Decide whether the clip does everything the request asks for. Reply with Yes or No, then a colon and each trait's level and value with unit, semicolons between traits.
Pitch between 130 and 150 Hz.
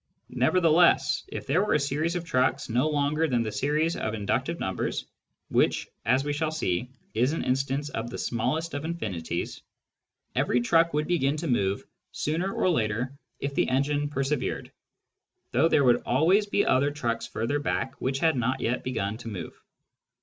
Yes: medium, 140 Hz